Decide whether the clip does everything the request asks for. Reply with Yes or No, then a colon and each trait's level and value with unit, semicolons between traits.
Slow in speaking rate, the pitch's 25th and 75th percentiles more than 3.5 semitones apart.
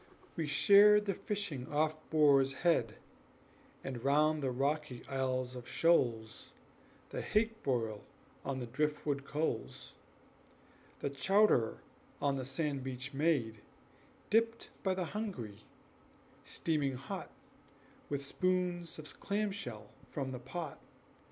Yes: slow, 120 wpm; average, 5.1 semitones